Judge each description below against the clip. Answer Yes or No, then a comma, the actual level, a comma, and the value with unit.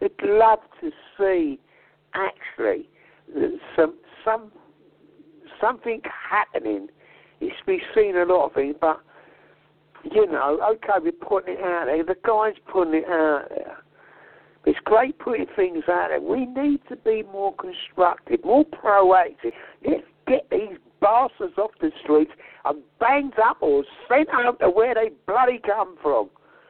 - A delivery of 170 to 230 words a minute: No, average, 145 wpm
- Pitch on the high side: Yes, very high, 260 Hz